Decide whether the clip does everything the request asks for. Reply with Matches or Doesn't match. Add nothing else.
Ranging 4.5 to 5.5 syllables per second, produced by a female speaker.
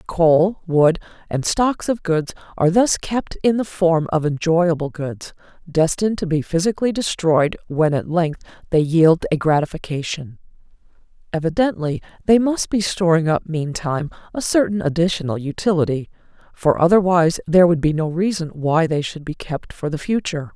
Matches